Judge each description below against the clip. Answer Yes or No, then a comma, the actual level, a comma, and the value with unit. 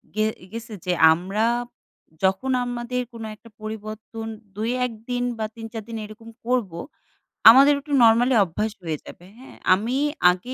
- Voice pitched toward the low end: No, high, 225 Hz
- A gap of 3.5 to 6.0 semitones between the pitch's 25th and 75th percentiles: No, narrow, 2.6 semitones